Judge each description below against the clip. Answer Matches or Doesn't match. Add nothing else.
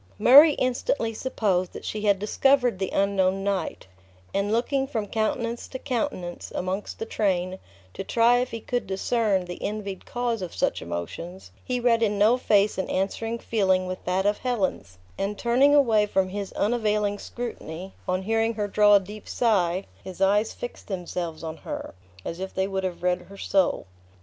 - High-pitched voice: Matches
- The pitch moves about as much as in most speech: Matches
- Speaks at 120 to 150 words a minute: Doesn't match